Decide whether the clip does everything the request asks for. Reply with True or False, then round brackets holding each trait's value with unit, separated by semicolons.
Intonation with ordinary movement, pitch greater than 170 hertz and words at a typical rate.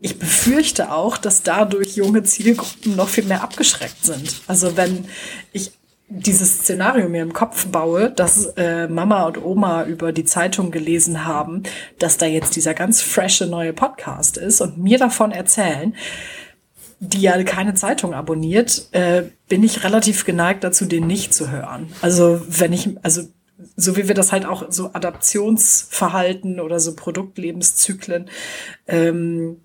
True (3.4 semitones; 185 Hz; 150 wpm)